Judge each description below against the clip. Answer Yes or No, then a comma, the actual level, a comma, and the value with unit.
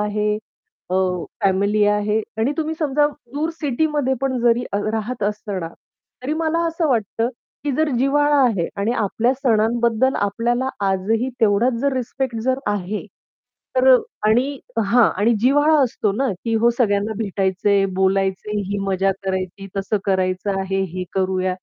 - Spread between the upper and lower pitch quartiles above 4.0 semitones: Yes, average, 4.8 semitones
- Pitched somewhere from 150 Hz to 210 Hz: No, high, 220 Hz